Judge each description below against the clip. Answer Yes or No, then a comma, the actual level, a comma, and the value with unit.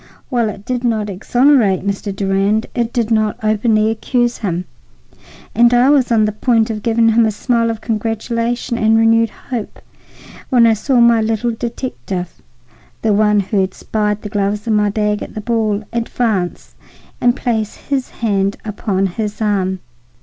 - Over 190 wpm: No, average, 160 wpm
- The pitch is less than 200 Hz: No, high, 220 Hz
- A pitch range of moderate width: No, narrow, 2.3 semitones